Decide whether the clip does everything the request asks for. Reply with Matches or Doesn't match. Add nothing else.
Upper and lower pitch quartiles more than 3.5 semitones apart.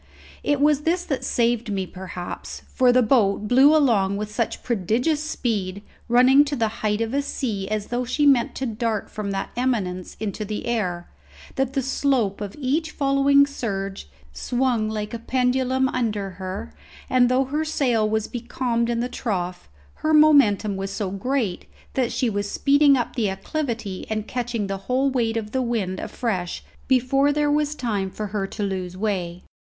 Matches